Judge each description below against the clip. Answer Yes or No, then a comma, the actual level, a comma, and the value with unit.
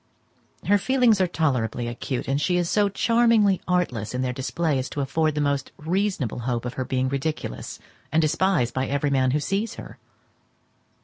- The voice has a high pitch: No, medium, 150 Hz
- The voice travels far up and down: Yes, wide, 6.2 semitones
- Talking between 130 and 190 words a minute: Yes, average, 180 wpm